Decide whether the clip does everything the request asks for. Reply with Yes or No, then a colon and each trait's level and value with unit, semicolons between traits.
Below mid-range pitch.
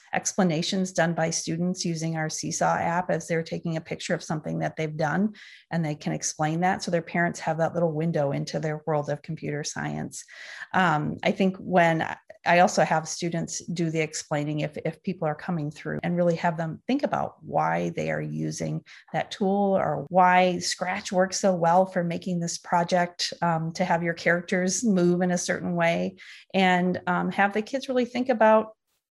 No: medium, 170 Hz